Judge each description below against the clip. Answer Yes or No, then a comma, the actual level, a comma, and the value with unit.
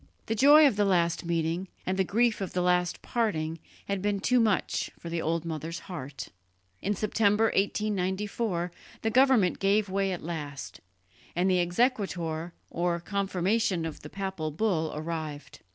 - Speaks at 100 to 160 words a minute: Yes, average, 155 wpm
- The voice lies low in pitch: No, medium, 185 Hz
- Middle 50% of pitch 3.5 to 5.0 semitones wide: Yes, average, 3.8 semitones